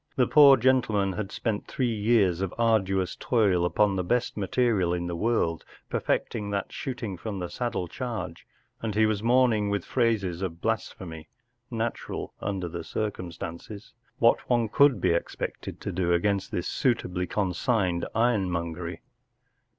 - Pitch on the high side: No, low, 100 Hz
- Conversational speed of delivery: Yes, average, 150 wpm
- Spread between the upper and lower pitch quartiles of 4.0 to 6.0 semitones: Yes, average, 4.5 semitones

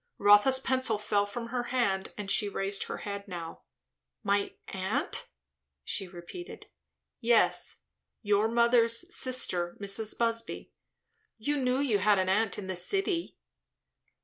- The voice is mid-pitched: No, high, 210 Hz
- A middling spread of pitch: Yes, average, 3.6 semitones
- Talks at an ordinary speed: No, slow, 130 wpm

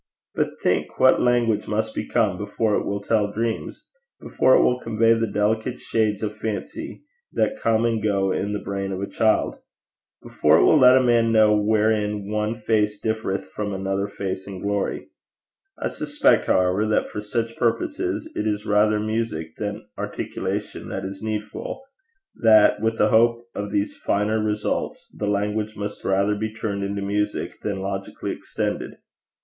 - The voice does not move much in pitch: Yes, narrow, 1.7 semitones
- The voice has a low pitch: Yes, low, 105 Hz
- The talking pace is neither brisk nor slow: Yes, average, 165 wpm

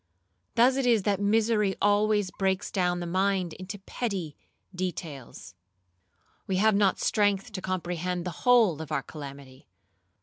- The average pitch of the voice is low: No, high, 190 Hz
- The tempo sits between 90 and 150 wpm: Yes, average, 140 wpm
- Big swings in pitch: No, average, 3.0 semitones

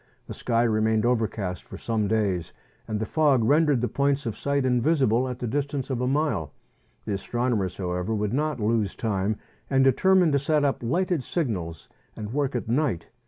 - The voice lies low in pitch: Yes, low, 120 Hz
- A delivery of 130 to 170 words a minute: No, average, 180 wpm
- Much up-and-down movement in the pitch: No, average, 4.8 semitones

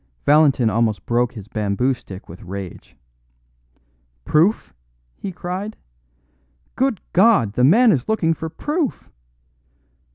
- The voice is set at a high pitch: No, low, 135 Hz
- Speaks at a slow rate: Yes, slow, 110 wpm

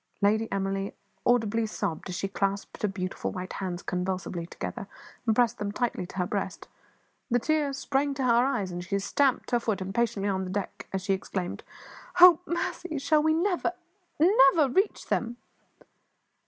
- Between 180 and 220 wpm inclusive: No, average, 170 wpm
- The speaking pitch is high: Yes, high, 210 Hz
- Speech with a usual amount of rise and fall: No, wide, 6.0 semitones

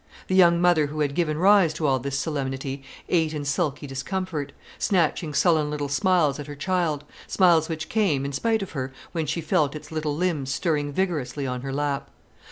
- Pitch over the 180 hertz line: No, medium, 155 Hz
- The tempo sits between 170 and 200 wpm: Yes, average, 190 wpm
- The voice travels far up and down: No, average, 3.6 semitones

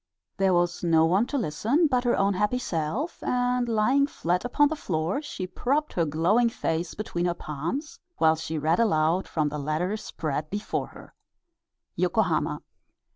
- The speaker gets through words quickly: No, average, 165 wpm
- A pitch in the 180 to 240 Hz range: Yes, medium, 185 Hz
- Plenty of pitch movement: Yes, wide, 7.4 semitones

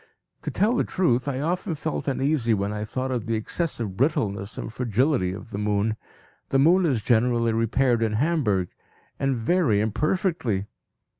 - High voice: No, low, 120 Hz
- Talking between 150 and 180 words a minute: Yes, average, 160 wpm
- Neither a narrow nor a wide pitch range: No, wide, 5.8 semitones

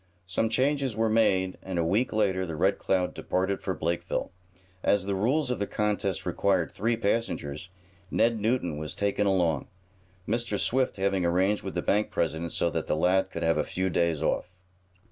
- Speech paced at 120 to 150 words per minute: No, average, 185 wpm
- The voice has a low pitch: Yes, very low, 95 Hz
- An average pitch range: Yes, average, 3.7 semitones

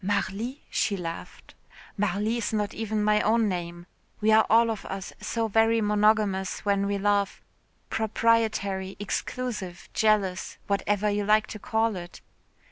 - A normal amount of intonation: No, narrow, 2.0 semitones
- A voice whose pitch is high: Yes, high, 210 Hz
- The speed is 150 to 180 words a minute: No, average, 140 wpm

